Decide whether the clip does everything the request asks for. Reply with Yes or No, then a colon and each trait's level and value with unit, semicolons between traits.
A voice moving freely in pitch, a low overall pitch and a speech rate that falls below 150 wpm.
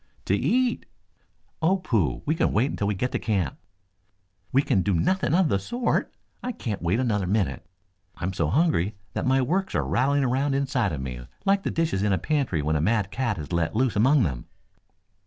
No: wide, 7.5 semitones; low, 115 Hz; average, 200 wpm